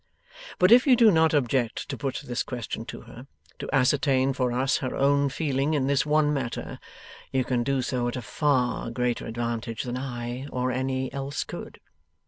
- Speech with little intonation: Yes, narrow, 2.3 semitones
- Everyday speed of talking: Yes, average, 185 wpm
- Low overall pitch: Yes, low, 130 Hz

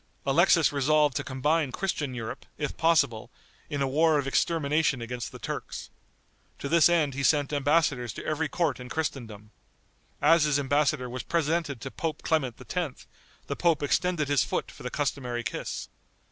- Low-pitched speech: No, medium, 145 Hz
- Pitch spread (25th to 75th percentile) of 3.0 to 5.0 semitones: Yes, average, 3.6 semitones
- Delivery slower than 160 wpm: No, average, 165 wpm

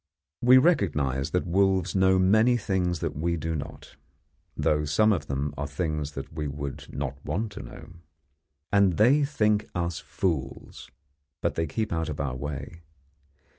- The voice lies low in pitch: Yes, very low, 85 Hz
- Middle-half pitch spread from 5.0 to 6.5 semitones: Yes, wide, 5.4 semitones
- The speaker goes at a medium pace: Yes, average, 160 wpm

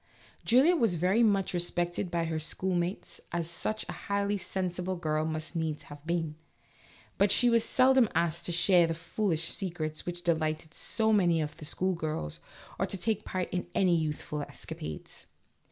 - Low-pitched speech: No, medium, 175 Hz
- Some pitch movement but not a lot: Yes, average, 3.5 semitones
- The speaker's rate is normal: Yes, average, 165 wpm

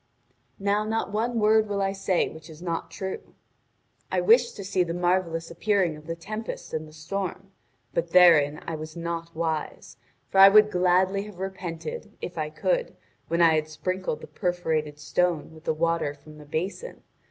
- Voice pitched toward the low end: No, medium, 175 Hz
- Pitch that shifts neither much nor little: Yes, average, 3.6 semitones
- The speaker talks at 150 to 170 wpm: No, average, 180 wpm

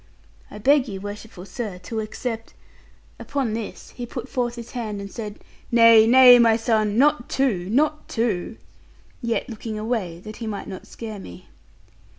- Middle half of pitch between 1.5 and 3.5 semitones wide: Yes, narrow, 2.6 semitones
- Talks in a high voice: Yes, high, 225 Hz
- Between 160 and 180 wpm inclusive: Yes, average, 165 wpm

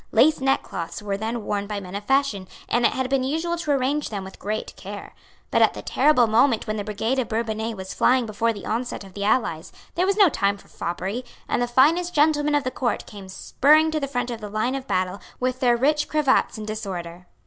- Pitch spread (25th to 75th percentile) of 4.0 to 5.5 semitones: Yes, average, 5.0 semitones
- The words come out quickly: Yes, fast, 230 wpm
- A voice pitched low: No, high, 235 Hz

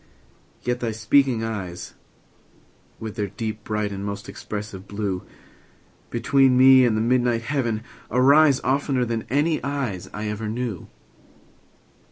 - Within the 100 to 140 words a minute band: Yes, slow, 135 wpm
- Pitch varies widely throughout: No, average, 3.6 semitones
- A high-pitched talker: No, low, 115 Hz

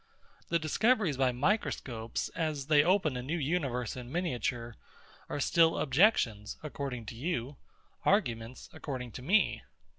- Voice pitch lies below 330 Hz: Yes, medium, 140 Hz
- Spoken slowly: Yes, slow, 130 wpm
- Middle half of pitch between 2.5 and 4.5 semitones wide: No, average, 5.3 semitones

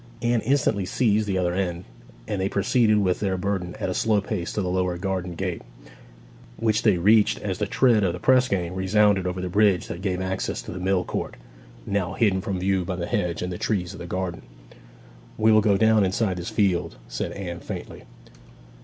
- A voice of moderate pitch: No, very low, 95 Hz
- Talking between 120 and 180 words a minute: No, fast, 205 wpm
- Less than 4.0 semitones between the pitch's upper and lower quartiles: Yes, narrow, 2.6 semitones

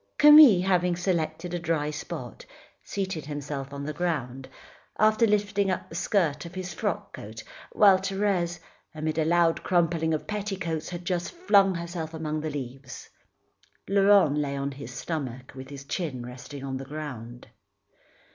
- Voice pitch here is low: No, medium, 165 Hz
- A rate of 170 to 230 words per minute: No, average, 155 wpm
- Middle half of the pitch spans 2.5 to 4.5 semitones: No, average, 4.9 semitones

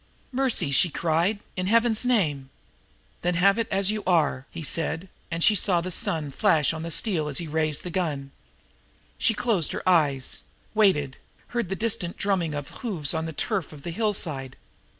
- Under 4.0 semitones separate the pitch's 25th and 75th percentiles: No, average, 5.0 semitones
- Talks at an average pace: Yes, average, 185 wpm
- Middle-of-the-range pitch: Yes, medium, 170 Hz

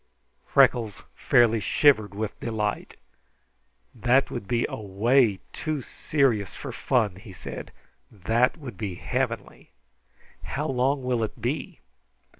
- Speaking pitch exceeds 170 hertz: No, low, 115 Hz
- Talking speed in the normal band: No, slow, 115 wpm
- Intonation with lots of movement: No, average, 3.8 semitones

